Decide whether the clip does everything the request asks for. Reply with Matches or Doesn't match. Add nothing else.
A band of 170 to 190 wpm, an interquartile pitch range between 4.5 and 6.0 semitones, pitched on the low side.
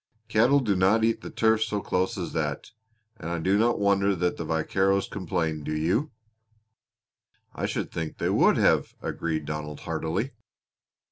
Doesn't match